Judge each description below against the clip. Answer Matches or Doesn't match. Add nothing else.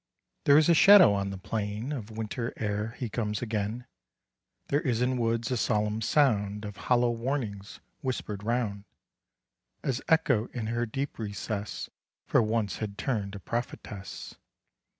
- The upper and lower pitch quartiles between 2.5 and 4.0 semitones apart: Matches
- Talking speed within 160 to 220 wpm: Doesn't match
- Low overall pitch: Matches